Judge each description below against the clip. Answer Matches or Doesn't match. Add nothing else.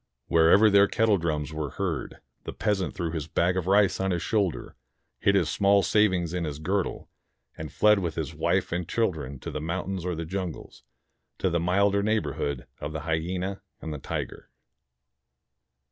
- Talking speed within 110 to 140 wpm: Doesn't match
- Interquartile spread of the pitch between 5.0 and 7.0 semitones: Doesn't match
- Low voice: Matches